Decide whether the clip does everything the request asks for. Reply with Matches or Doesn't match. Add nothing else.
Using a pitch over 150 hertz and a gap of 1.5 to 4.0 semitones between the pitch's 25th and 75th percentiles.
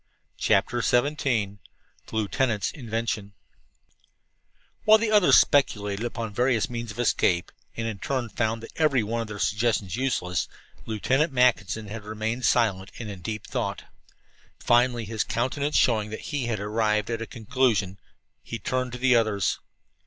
Doesn't match